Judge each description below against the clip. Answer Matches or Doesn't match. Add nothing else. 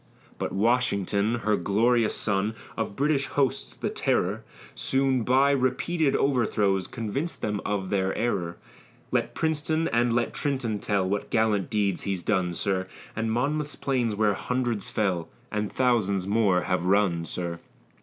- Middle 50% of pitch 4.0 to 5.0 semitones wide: Matches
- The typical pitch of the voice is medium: Doesn't match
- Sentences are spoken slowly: Doesn't match